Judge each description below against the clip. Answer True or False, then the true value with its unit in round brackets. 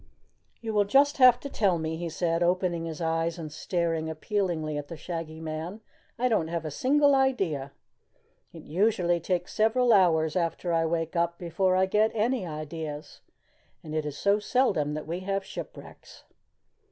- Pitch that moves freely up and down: False (4.3 semitones)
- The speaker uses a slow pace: False (170 wpm)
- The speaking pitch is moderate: True (170 Hz)